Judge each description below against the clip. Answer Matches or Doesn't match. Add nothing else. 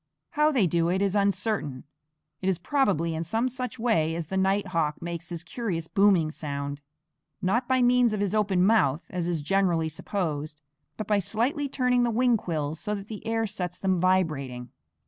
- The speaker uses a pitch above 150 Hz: Matches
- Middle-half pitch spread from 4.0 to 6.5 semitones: Matches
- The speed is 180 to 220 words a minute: Matches